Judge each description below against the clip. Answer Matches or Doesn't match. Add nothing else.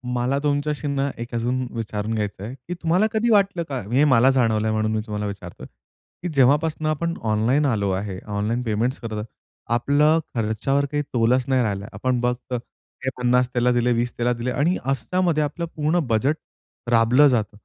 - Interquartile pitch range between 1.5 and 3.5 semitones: Doesn't match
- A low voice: Matches